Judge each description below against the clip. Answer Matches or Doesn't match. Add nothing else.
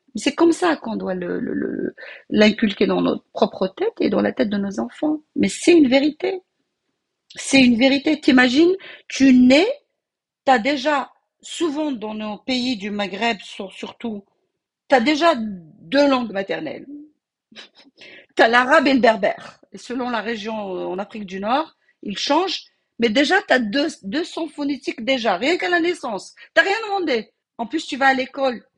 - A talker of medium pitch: Doesn't match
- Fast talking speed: Doesn't match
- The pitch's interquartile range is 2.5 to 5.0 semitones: Doesn't match